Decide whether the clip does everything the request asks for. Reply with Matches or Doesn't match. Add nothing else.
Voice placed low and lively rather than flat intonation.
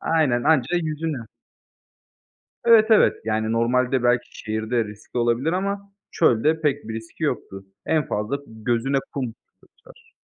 Matches